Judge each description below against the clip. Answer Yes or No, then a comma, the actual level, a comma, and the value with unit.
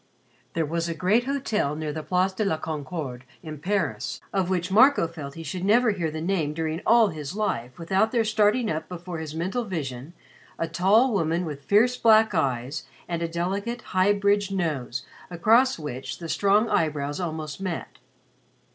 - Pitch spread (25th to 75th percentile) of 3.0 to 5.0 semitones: Yes, average, 4.7 semitones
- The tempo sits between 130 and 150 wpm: No, average, 175 wpm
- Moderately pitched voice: Yes, medium, 175 Hz